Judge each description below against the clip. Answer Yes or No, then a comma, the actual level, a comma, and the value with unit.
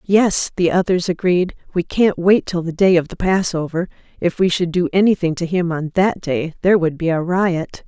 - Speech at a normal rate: No, fast, 215 wpm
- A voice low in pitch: No, medium, 175 Hz